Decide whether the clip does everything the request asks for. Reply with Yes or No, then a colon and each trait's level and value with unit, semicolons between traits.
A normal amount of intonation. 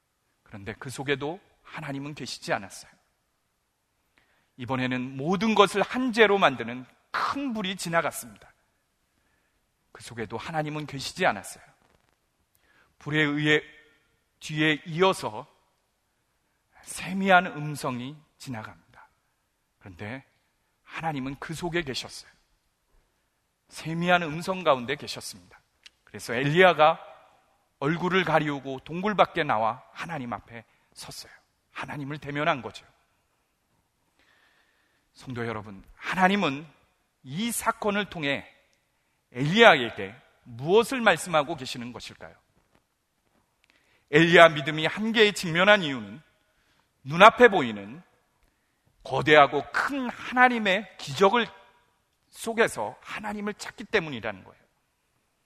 No: wide, 6.0 semitones